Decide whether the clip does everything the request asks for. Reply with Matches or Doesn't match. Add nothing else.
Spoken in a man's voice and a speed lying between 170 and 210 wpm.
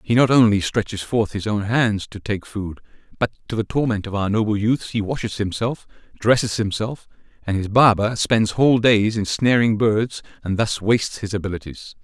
Matches